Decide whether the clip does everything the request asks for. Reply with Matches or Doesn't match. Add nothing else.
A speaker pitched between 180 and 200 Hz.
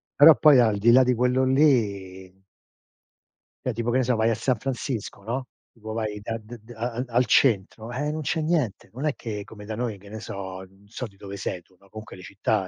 Doesn't match